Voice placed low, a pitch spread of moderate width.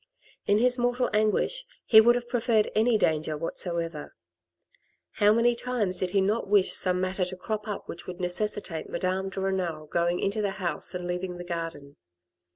No: high, 190 Hz; average, 3.5 semitones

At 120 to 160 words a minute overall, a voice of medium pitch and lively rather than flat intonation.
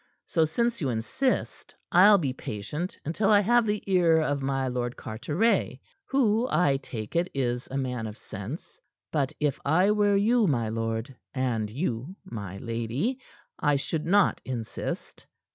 Yes: average, 155 wpm; medium, 145 Hz; wide, 8.4 semitones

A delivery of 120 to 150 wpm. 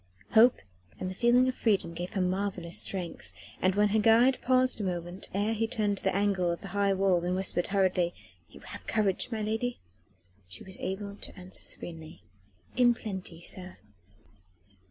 No: average, 175 wpm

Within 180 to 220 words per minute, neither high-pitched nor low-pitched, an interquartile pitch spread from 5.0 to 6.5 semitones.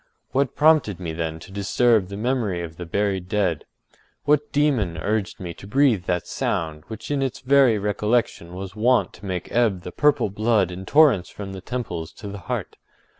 No: average, 185 wpm; low, 100 Hz; average, 5.3 semitones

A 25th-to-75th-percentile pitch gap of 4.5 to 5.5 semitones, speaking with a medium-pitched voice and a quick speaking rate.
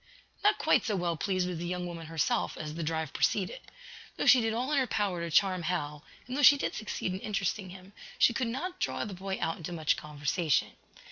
Yes: average, 4.9 semitones; medium, 180 Hz; fast, 225 wpm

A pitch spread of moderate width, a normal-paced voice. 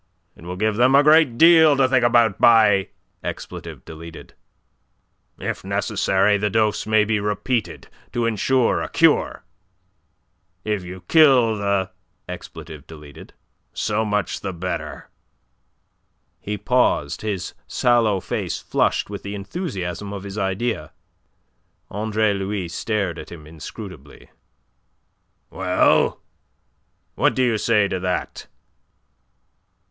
No: average, 3.4 semitones; slow, 110 wpm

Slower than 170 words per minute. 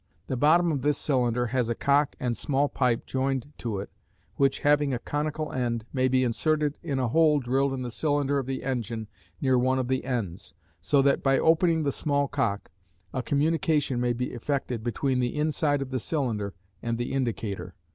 No: average, 195 wpm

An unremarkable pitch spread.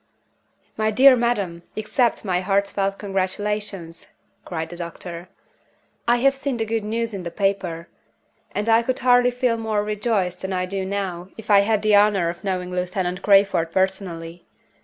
Yes: average, 3.3 semitones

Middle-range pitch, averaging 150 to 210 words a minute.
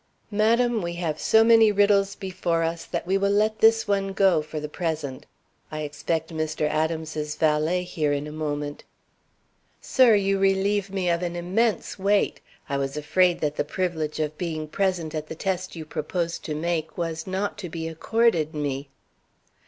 Yes: medium, 170 Hz; average, 175 wpm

